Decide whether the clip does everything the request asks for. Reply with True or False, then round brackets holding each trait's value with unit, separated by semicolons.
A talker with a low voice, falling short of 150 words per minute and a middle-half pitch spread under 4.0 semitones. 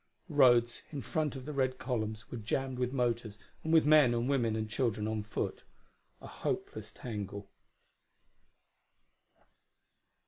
True (120 Hz; 140 wpm; 3.5 semitones)